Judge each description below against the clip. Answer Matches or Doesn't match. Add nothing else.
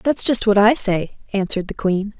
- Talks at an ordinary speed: Doesn't match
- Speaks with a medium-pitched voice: Doesn't match